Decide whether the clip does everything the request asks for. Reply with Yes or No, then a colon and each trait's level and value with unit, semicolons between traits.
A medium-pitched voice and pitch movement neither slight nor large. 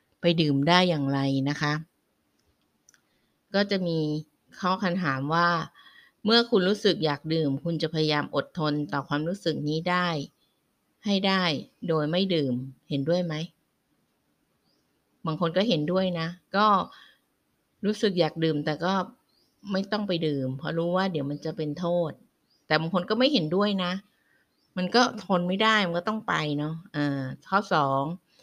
Yes: medium, 170 Hz; average, 3.9 semitones